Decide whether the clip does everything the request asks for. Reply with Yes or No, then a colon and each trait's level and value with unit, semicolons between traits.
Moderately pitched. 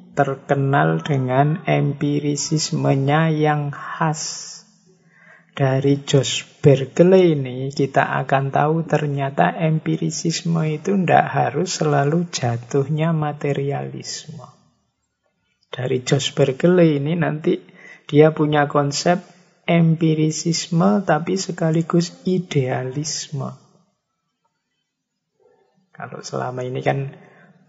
Yes: medium, 155 Hz